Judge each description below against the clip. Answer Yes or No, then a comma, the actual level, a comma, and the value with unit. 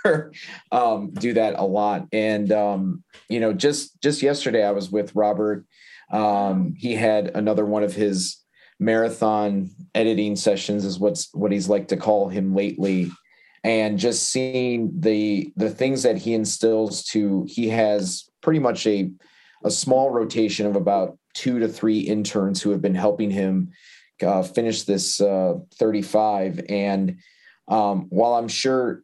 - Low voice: Yes, low, 105 Hz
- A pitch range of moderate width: No, narrow, 2.1 semitones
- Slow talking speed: No, average, 155 wpm